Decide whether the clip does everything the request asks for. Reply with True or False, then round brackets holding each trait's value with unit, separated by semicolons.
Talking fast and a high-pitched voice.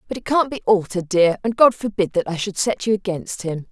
True (260 wpm; 200 Hz)